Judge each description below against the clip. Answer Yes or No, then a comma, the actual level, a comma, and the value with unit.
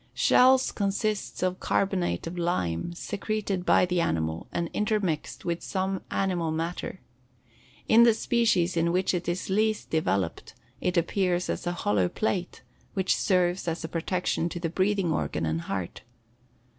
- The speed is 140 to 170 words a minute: Yes, average, 150 wpm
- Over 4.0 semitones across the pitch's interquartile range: No, average, 2.9 semitones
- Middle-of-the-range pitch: Yes, medium, 180 Hz